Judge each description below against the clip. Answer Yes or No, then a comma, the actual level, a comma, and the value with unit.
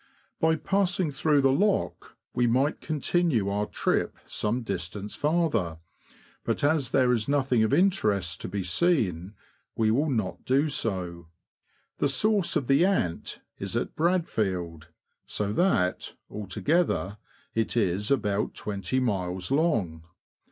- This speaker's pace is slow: Yes, slow, 130 wpm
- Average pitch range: No, wide, 7.8 semitones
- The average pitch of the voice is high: No, low, 120 Hz